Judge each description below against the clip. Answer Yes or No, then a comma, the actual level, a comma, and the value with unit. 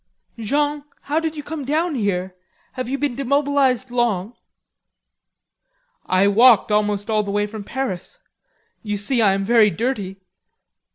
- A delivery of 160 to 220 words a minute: No, average, 145 wpm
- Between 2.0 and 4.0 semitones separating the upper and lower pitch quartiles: No, average, 5.3 semitones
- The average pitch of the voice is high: Yes, high, 235 Hz